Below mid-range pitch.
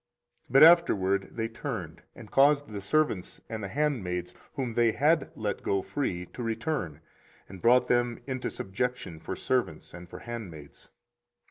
Yes: low, 115 Hz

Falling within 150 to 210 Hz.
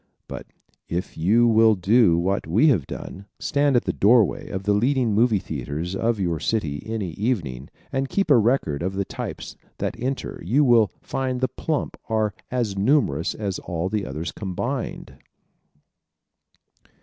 No: low, 105 Hz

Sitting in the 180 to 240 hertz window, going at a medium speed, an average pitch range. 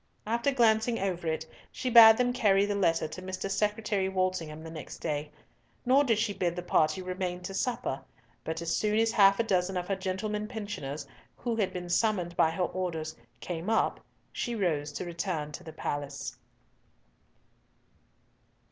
Yes: medium, 185 Hz; average, 170 wpm; average, 4.6 semitones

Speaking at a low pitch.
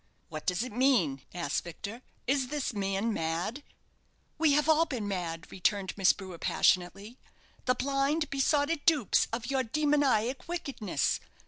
No: high, 240 Hz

